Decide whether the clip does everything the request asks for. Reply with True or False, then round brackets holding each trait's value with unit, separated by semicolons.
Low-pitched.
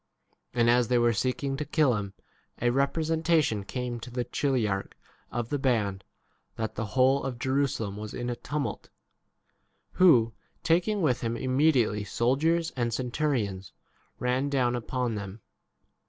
True (125 Hz)